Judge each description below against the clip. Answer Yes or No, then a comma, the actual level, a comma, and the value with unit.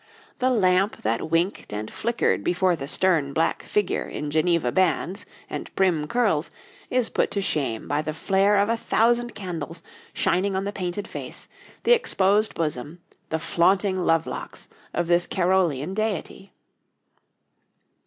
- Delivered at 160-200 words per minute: No, average, 145 wpm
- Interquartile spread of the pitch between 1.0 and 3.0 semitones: No, average, 4.0 semitones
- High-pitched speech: No, medium, 180 Hz